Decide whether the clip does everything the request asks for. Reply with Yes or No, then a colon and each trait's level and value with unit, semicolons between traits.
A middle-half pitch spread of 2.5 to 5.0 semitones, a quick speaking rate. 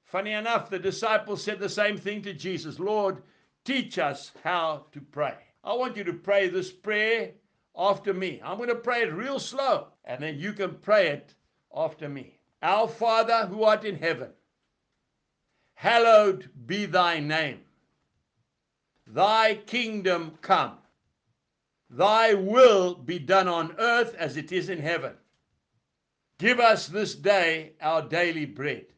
No: average, 4.7 semitones; average, 145 wpm